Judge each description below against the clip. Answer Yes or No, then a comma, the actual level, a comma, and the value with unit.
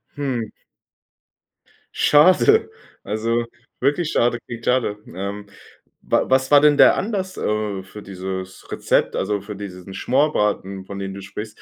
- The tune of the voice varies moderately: No, wide, 5.8 semitones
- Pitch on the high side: No, low, 105 Hz